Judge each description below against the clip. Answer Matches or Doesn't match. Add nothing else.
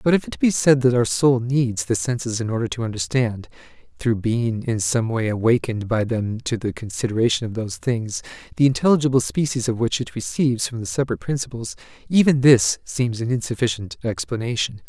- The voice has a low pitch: Matches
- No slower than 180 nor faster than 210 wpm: Matches